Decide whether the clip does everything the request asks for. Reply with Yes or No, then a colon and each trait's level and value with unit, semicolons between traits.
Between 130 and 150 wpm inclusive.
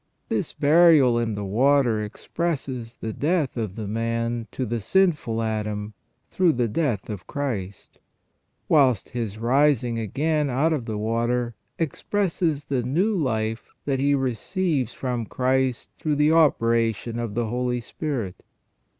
Yes: average, 140 wpm